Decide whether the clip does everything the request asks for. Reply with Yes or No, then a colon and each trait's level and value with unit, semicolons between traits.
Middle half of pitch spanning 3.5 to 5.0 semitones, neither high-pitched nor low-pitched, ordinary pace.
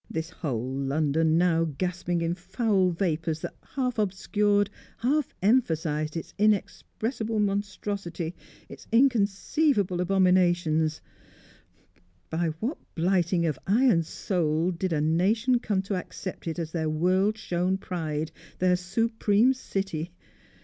No: average, 4.1 semitones; medium, 180 Hz; slow, 120 wpm